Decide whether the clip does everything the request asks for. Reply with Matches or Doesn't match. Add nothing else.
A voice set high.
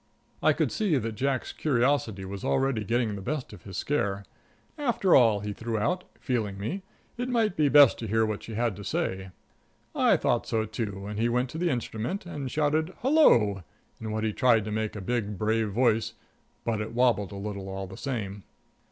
Doesn't match